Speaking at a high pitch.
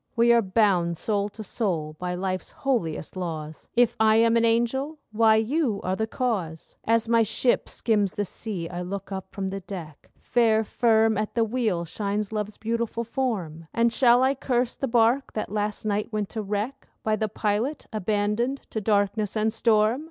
Yes: high, 215 Hz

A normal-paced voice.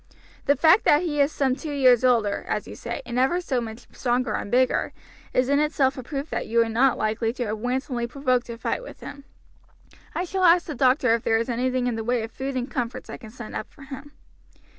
No: fast, 240 wpm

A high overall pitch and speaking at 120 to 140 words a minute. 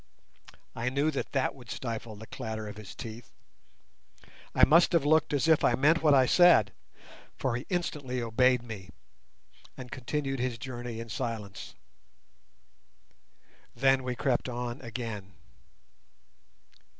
No: low, 125 Hz; slow, 135 wpm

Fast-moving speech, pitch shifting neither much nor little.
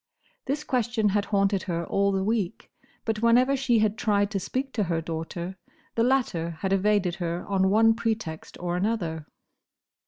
No: average, 165 wpm; average, 4.1 semitones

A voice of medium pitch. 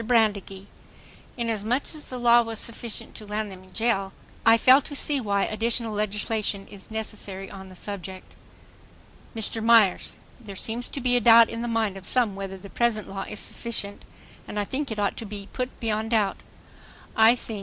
No: high, 220 Hz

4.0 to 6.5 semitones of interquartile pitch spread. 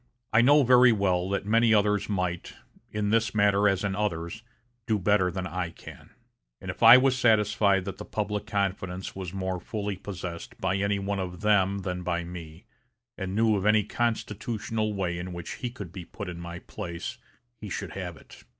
No: average, 2.8 semitones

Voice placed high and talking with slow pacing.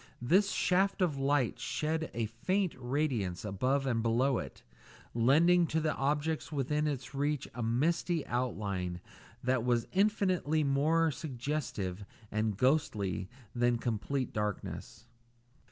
No: low, 135 Hz; slow, 120 wpm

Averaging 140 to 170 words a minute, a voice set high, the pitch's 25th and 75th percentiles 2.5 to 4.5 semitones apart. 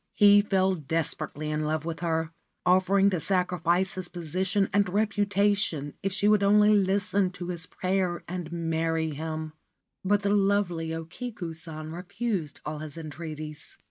No: average, 150 wpm; medium, 180 Hz; average, 3.6 semitones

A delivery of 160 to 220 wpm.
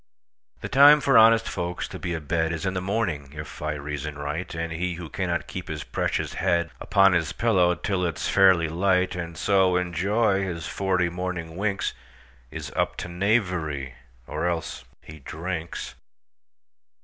No: average, 150 wpm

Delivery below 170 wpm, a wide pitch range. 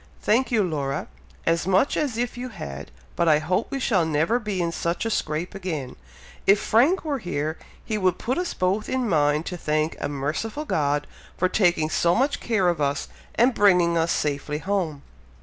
No: average, 190 wpm; wide, 6.3 semitones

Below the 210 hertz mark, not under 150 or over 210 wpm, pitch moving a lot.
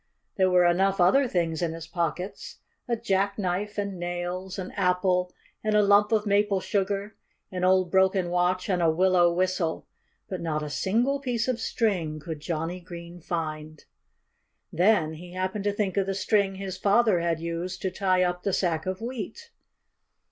No: medium, 185 Hz; average, 170 wpm; narrow, 2.5 semitones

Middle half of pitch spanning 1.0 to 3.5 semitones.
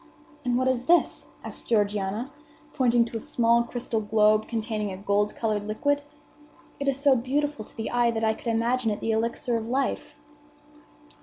Yes: average, 2.8 semitones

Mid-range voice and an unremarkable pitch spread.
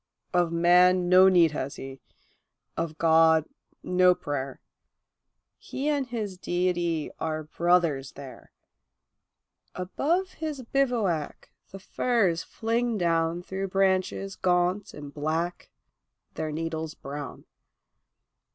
Yes: medium, 175 Hz; average, 3.3 semitones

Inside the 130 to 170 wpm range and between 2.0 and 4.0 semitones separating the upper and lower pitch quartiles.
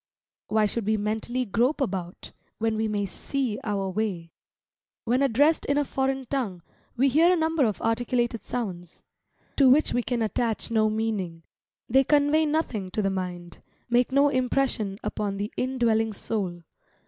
No: average, 160 wpm; average, 4.6 semitones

